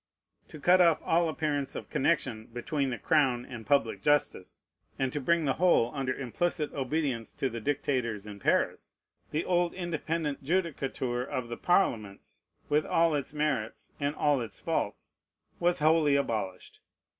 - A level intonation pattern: No, average, 4.6 semitones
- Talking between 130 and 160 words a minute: Yes, average, 155 wpm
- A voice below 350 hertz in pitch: Yes, medium, 140 Hz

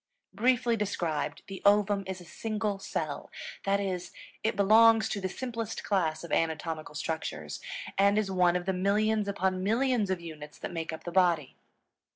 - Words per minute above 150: Yes, average, 170 wpm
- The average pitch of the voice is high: Yes, high, 195 Hz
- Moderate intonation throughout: Yes, average, 3.7 semitones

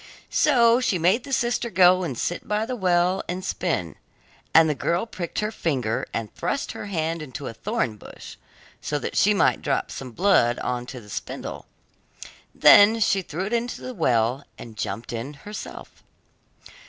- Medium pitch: Yes, medium, 175 Hz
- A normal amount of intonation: No, wide, 8.4 semitones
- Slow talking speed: No, average, 175 wpm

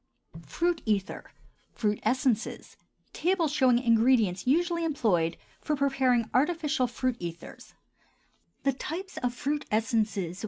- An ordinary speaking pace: No, slow, 95 wpm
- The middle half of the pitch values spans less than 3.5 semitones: No, wide, 5.4 semitones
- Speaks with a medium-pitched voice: No, very high, 255 Hz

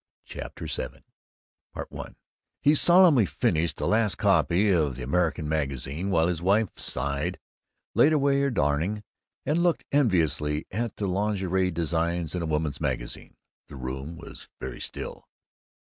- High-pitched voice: No, very low, 85 Hz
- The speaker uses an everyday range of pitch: No, wide, 5.9 semitones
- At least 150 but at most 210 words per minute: No, average, 140 wpm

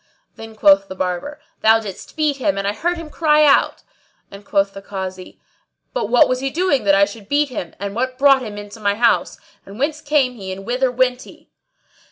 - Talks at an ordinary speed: No, fast, 220 wpm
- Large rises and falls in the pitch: Yes, wide, 6.0 semitones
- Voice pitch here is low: No, high, 230 Hz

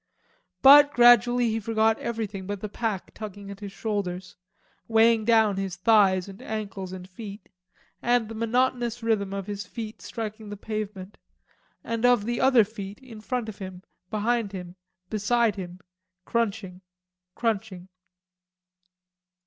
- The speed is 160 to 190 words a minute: No, average, 140 wpm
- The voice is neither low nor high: No, high, 215 Hz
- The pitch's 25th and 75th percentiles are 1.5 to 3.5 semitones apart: Yes, average, 2.8 semitones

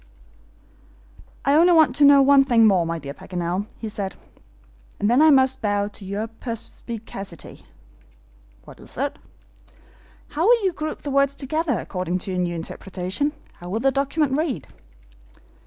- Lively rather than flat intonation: Yes, wide, 6.9 semitones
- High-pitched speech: Yes, high, 230 Hz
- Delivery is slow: No, average, 155 wpm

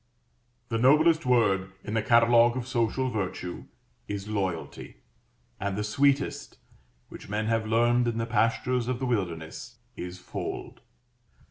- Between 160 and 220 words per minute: No, slow, 135 wpm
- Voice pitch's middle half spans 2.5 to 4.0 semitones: Yes, average, 3.2 semitones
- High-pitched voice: No, low, 115 Hz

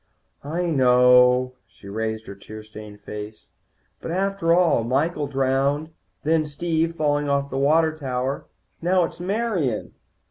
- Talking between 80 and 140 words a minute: Yes, slow, 135 wpm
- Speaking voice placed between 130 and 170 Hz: Yes, medium, 140 Hz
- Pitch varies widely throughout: No, average, 4.7 semitones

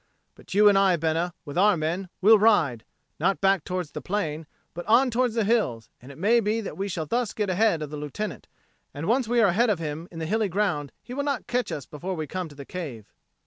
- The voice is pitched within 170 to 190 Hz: Yes, medium, 185 Hz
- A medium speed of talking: No, fast, 245 wpm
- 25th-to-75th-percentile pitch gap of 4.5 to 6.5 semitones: Yes, wide, 5.6 semitones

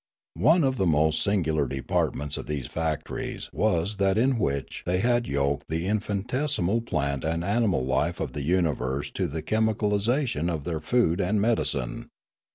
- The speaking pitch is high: No, very low, 90 Hz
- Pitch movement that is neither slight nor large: No, wide, 6.4 semitones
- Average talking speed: Yes, average, 170 wpm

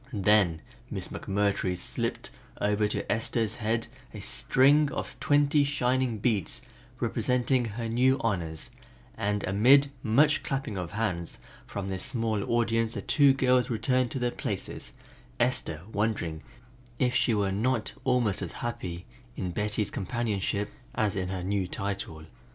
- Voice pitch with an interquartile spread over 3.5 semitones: Yes, average, 4.3 semitones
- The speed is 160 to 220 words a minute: No, slow, 135 wpm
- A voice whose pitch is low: Yes, low, 110 Hz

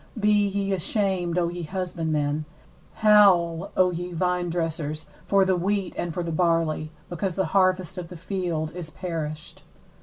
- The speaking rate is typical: Yes, average, 150 wpm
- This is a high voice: No, medium, 175 Hz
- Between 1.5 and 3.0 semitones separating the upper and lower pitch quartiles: Yes, narrow, 2.5 semitones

